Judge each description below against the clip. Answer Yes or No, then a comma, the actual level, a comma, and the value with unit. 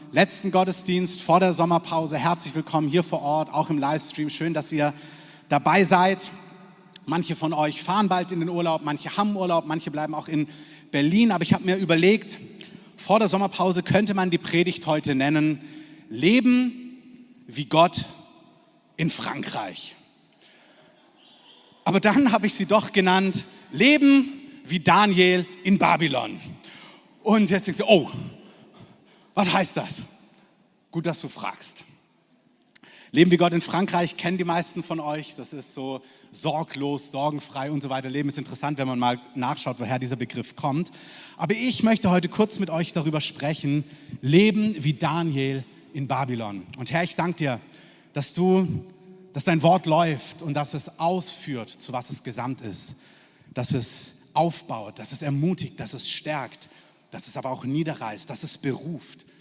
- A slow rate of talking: No, average, 160 wpm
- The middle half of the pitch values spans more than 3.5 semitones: Yes, average, 4.1 semitones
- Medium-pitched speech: Yes, medium, 165 Hz